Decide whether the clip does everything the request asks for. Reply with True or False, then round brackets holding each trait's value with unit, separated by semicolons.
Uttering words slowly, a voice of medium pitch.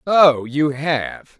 True (130 wpm; 145 Hz)